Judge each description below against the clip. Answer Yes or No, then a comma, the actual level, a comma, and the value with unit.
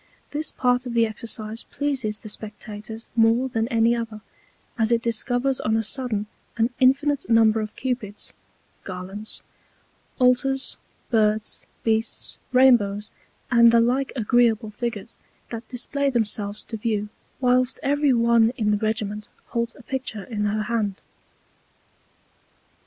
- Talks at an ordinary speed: No, slow, 130 wpm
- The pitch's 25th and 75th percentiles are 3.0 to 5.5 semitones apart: No, narrow, 2.6 semitones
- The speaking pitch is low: No, high, 230 Hz